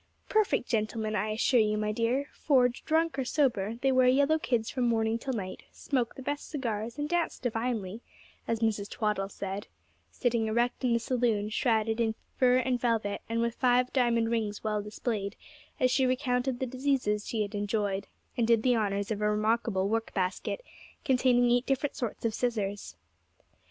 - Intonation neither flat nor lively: Yes, average, 3.0 semitones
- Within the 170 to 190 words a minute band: Yes, average, 175 wpm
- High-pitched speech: Yes, high, 230 Hz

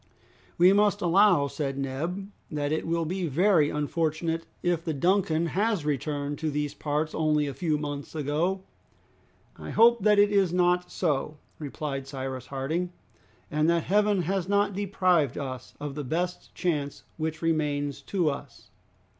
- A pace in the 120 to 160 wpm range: Yes, average, 155 wpm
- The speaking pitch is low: No, medium, 160 Hz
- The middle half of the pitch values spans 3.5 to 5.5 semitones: Yes, average, 3.8 semitones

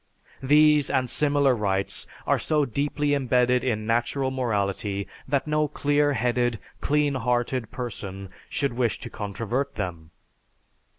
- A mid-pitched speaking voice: No, low, 125 Hz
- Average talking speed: No, slow, 125 wpm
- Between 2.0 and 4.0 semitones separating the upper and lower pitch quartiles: No, average, 4.7 semitones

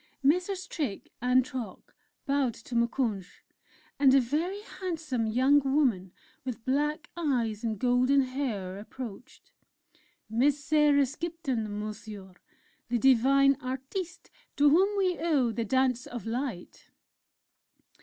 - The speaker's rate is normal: No, slow, 115 wpm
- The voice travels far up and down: No, average, 4.1 semitones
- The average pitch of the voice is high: Yes, very high, 260 Hz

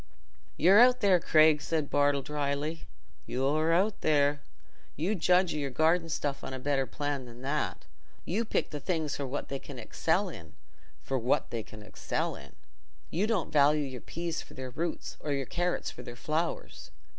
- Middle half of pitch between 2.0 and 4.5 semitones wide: Yes, average, 3.3 semitones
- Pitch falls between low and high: Yes, medium, 150 Hz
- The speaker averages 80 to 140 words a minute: No, average, 180 wpm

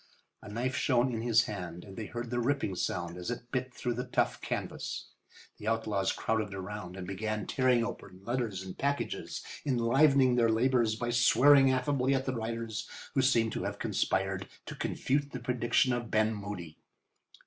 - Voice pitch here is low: Yes, low, 115 Hz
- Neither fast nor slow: Yes, average, 175 wpm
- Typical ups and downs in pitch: Yes, average, 3.5 semitones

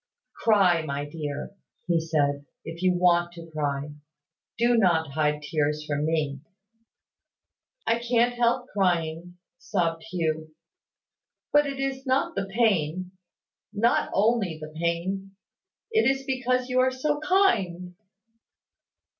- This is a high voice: No, medium, 180 Hz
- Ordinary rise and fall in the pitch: No, wide, 7.1 semitones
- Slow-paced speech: Yes, slow, 120 wpm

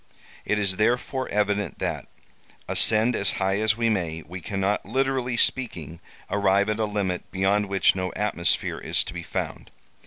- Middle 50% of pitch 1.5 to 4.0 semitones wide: Yes, narrow, 2.5 semitones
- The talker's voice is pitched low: Yes, low, 105 Hz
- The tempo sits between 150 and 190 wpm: Yes, average, 160 wpm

